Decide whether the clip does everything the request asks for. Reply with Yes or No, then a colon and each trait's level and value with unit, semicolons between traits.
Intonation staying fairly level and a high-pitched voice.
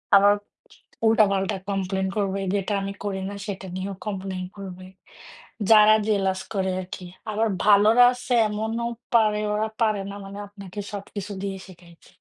Yes: narrow, 1.7 semitones; high, 200 Hz